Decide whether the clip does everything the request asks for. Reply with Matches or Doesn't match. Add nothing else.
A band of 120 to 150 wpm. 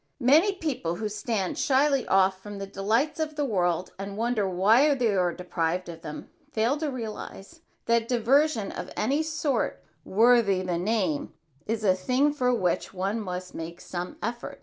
Doesn't match